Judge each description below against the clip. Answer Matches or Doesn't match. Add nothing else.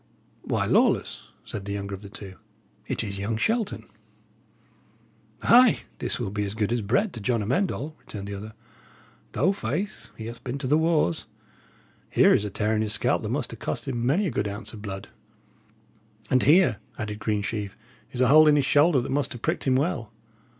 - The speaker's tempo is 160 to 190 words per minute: Doesn't match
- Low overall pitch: Matches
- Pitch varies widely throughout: Matches